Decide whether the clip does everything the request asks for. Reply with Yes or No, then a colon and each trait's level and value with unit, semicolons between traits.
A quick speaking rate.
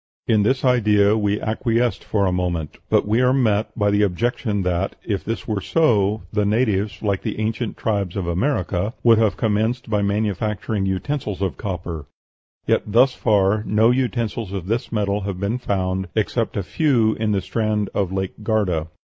No: average, 175 wpm